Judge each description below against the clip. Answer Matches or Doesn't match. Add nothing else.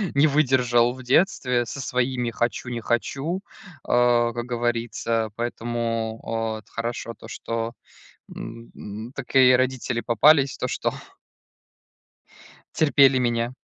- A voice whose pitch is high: Doesn't match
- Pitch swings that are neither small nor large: Doesn't match